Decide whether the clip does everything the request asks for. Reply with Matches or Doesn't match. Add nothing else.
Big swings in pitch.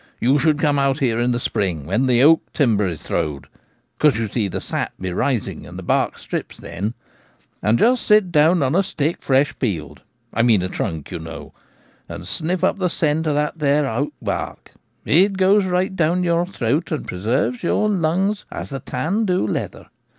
Matches